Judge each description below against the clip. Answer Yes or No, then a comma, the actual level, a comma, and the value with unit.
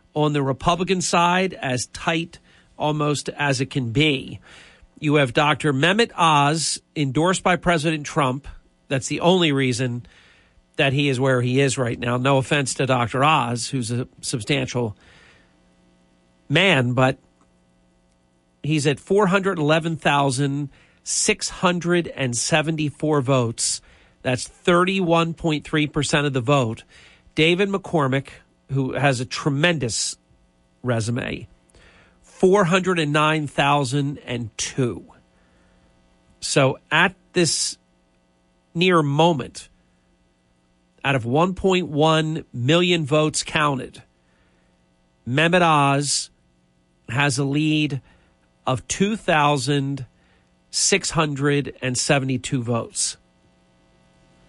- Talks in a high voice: No, medium, 140 Hz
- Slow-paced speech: Yes, slow, 85 wpm